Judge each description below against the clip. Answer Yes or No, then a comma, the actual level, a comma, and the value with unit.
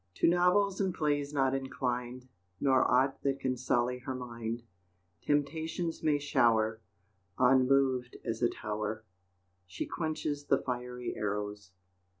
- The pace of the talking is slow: Yes, slow, 125 wpm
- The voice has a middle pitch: No, low, 130 Hz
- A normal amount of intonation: Yes, average, 3.4 semitones